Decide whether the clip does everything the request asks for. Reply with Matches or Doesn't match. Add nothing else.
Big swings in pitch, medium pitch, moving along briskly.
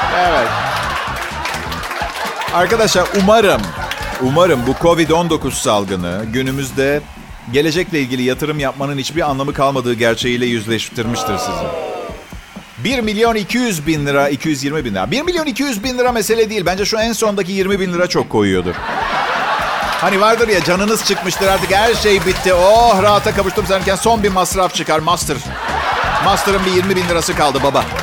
Matches